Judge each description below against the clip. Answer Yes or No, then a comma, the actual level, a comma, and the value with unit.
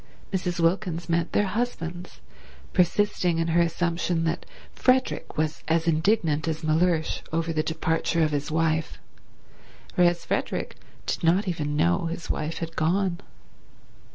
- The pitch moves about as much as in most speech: No, narrow, 1.7 semitones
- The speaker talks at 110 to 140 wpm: Yes, slow, 135 wpm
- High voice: No, medium, 165 Hz